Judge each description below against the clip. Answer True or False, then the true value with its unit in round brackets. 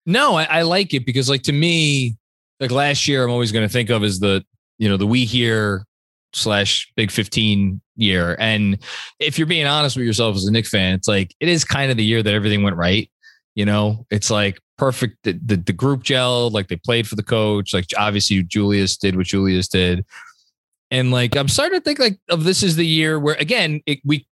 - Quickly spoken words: True (225 wpm)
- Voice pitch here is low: True (115 Hz)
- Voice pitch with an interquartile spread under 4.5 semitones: False (5.6 semitones)